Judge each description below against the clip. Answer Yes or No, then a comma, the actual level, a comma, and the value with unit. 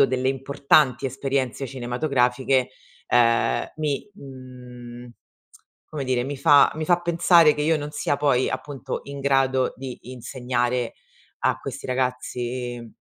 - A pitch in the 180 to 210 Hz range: No, low, 130 Hz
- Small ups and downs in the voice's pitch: Yes, narrow, 2.3 semitones